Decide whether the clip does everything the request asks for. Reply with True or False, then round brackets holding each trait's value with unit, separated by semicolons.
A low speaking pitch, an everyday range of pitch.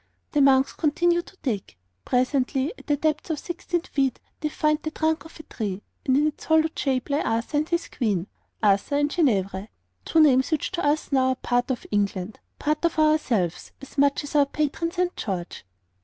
False (285 Hz; 4.1 semitones)